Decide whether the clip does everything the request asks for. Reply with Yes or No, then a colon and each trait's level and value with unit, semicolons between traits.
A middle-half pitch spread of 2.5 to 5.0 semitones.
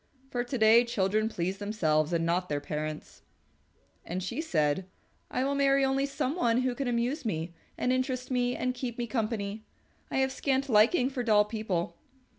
No: wide, 5.5 semitones